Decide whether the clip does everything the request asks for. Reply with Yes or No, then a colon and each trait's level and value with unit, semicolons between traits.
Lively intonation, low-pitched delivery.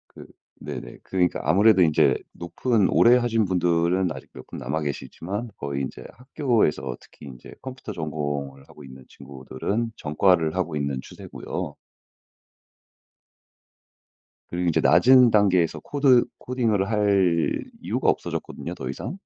Yes: wide, 7.1 semitones; very low, 90 Hz